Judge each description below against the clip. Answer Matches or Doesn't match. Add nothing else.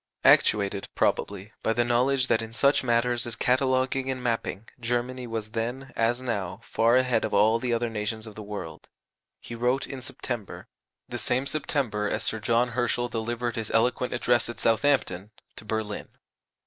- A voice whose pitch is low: Matches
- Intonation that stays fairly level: Matches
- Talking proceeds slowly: Doesn't match